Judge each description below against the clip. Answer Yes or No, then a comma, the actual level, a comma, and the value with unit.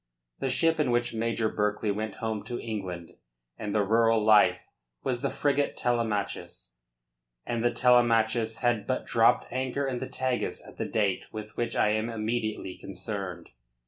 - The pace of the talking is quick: No, average, 160 wpm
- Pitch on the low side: Yes, low, 115 Hz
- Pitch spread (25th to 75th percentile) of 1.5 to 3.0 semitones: Yes, narrow, 2.4 semitones